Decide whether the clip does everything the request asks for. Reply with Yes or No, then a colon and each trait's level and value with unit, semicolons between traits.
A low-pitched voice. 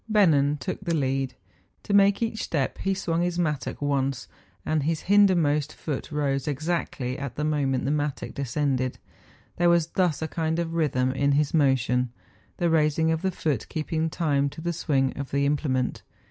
No: medium, 150 Hz